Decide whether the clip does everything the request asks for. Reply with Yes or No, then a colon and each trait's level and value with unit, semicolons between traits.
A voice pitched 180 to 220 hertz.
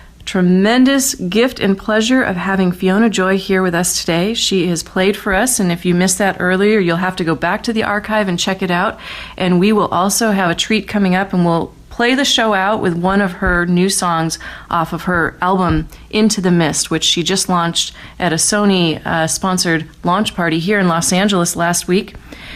Yes: medium, 185 Hz